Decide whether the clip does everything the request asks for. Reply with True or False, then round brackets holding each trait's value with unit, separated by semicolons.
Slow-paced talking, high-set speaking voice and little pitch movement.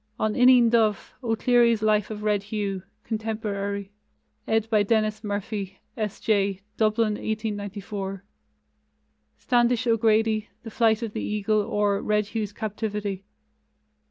True (120 wpm; 215 Hz; 1.7 semitones)